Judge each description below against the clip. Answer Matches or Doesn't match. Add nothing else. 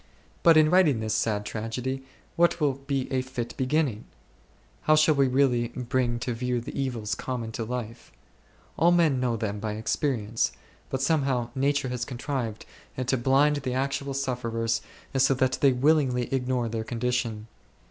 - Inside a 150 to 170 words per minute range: Matches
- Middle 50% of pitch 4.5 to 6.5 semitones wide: Doesn't match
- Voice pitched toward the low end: Matches